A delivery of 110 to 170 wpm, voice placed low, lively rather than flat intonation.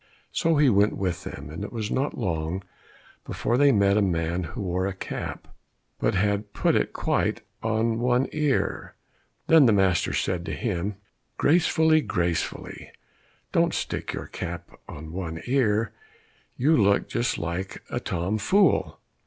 Yes: average, 155 wpm; low, 100 Hz; wide, 5.8 semitones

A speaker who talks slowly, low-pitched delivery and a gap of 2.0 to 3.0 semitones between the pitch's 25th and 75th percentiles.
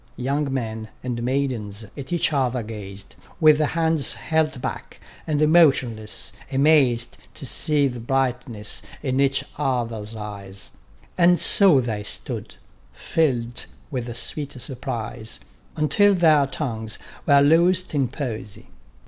No: slow, 125 wpm; low, 130 Hz; average, 4.8 semitones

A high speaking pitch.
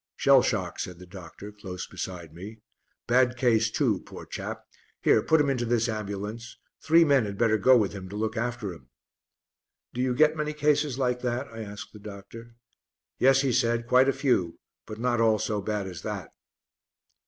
No: low, 115 Hz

